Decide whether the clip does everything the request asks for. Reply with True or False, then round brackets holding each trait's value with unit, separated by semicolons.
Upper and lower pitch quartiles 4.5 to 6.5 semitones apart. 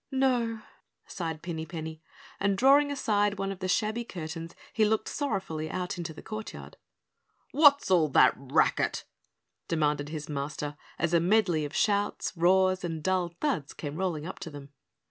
True (5.1 semitones)